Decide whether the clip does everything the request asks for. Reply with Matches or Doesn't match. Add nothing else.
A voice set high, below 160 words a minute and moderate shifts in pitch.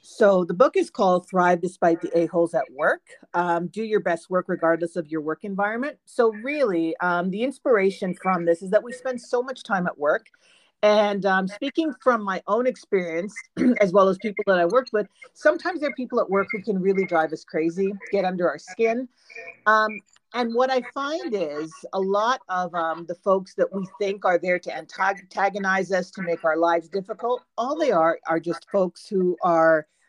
Doesn't match